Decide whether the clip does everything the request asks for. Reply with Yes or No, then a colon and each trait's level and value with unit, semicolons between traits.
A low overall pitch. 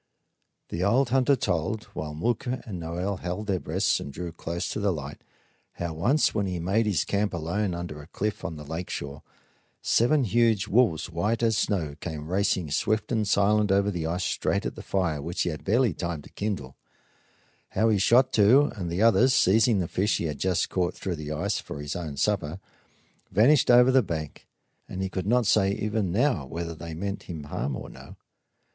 Yes: very low, 95 Hz